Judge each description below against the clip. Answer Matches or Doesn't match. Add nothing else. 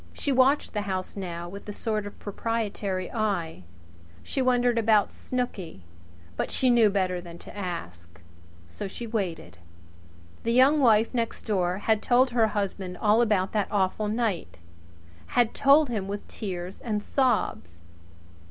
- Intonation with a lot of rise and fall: Doesn't match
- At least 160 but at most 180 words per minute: Doesn't match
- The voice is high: Matches